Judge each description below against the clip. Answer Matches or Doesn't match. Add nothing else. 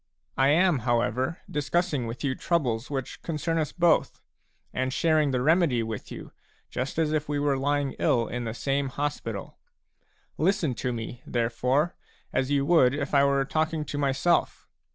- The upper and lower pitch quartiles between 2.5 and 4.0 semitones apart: Matches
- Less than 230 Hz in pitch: Matches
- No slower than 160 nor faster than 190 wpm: Matches